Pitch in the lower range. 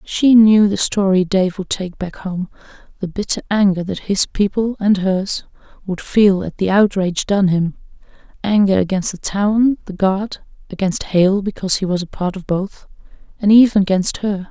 No: high, 195 Hz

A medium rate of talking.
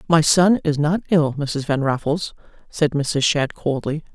Yes: average, 175 wpm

